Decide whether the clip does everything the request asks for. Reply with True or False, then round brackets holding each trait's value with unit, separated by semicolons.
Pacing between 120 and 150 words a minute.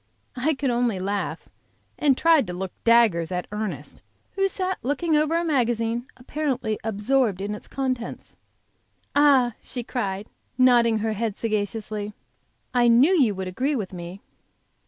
True (145 wpm)